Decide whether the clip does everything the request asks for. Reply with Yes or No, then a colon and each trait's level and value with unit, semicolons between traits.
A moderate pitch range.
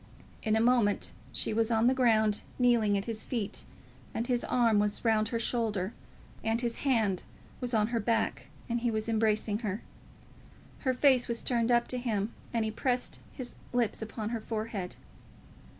No: narrow, 2.0 semitones